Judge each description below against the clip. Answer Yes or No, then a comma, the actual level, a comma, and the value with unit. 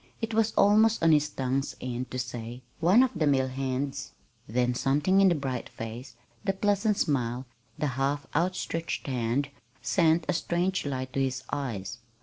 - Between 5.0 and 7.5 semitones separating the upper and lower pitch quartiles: Yes, average, 5.3 semitones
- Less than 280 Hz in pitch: Yes, medium, 140 Hz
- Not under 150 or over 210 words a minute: Yes, average, 165 wpm